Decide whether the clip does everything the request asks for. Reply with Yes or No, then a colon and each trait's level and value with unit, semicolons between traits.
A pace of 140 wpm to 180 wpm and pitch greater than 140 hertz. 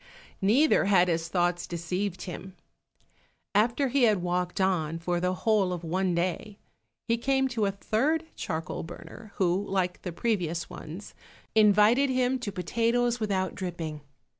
Yes: average, 145 wpm; high, 190 Hz